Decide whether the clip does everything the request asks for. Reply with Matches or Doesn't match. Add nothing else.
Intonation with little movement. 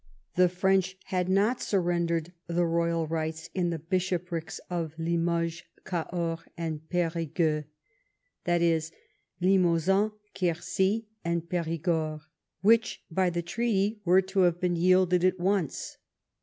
Matches